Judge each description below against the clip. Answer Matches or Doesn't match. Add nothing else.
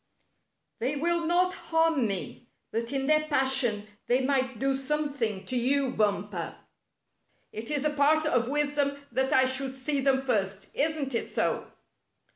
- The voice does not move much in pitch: Doesn't match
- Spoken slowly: Doesn't match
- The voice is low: Doesn't match